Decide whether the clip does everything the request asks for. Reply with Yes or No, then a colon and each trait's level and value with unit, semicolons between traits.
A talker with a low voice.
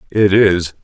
Yes: very low, 95 Hz